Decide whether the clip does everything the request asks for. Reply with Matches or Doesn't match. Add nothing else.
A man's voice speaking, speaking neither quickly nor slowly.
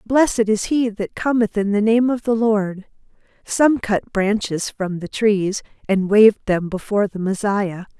Doesn't match